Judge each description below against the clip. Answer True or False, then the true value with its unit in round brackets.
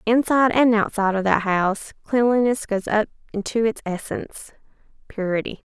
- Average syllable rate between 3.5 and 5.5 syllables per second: True (5.4 syllables/s)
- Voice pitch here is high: True (215 Hz)